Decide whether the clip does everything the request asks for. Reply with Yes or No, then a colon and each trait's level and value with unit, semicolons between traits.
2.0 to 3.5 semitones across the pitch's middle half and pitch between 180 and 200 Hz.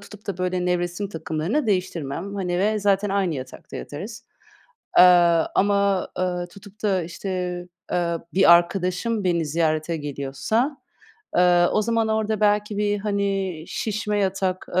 Yes: average, 3.1 semitones; high, 190 Hz